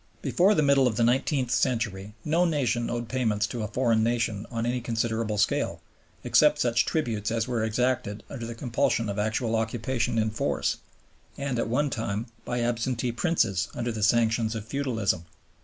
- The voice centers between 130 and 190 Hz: No, low, 115 Hz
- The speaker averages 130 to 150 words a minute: No, average, 175 wpm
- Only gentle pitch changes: Yes, narrow, 2.3 semitones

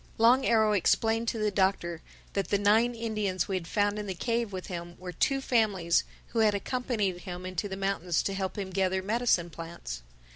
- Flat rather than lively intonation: No, average, 3.4 semitones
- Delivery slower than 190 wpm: No, average, 195 wpm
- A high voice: Yes, high, 200 Hz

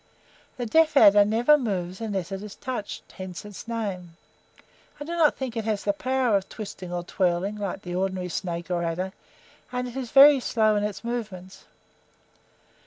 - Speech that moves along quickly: No, average, 175 wpm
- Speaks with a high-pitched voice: Yes, high, 205 Hz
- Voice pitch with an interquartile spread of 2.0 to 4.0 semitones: No, average, 4.6 semitones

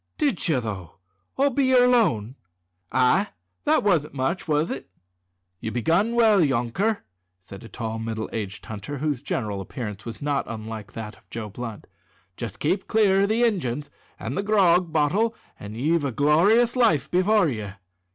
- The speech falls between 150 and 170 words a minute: Yes, average, 165 wpm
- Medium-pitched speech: Yes, medium, 145 Hz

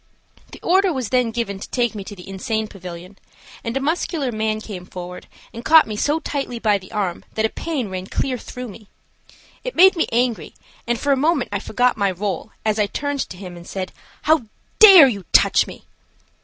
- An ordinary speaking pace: No, fast, 210 wpm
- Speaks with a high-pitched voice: Yes, high, 225 Hz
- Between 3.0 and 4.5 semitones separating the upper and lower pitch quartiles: No, wide, 5.5 semitones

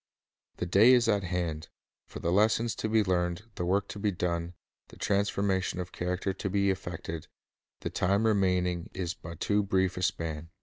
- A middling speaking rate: Yes, average, 190 wpm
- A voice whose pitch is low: Yes, very low, 95 Hz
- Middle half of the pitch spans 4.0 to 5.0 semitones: No, narrow, 2.4 semitones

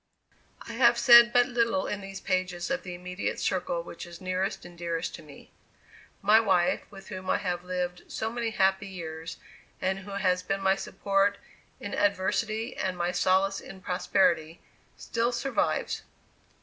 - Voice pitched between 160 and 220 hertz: Yes, high, 190 Hz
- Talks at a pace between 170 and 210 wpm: No, average, 160 wpm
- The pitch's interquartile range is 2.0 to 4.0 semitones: Yes, narrow, 2.5 semitones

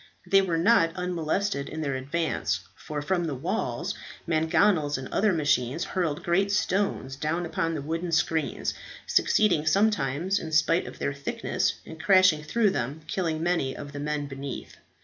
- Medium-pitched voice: Yes, medium, 160 Hz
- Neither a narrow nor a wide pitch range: Yes, average, 3.9 semitones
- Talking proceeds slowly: No, average, 160 wpm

